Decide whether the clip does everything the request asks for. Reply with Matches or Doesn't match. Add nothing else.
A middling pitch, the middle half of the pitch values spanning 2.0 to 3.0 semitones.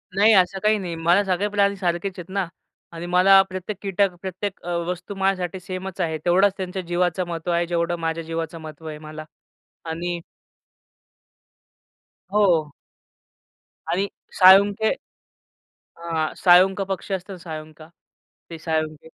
Matches